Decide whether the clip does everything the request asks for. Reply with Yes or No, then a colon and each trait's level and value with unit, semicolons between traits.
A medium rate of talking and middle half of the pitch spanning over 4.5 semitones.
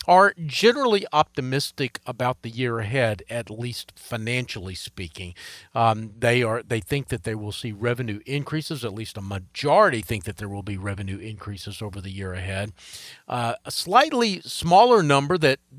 Yes: average, 165 wpm; average, 5.2 semitones